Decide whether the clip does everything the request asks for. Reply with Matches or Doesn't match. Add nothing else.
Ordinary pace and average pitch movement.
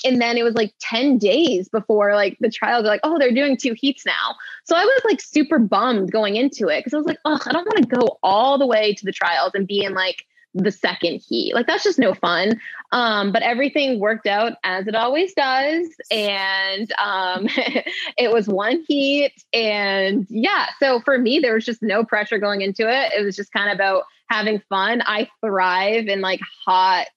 Doesn't match